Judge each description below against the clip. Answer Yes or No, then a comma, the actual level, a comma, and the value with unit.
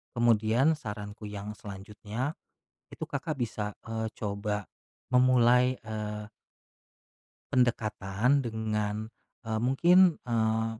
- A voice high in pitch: No, low, 110 Hz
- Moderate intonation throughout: Yes, average, 3.1 semitones